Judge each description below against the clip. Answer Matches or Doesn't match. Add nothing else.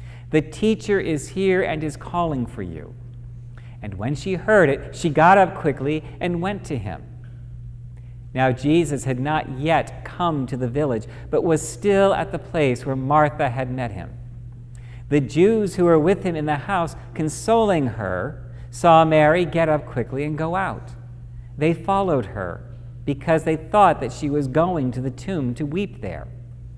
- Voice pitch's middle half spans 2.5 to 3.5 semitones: Doesn't match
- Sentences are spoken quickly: Doesn't match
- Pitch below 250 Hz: Matches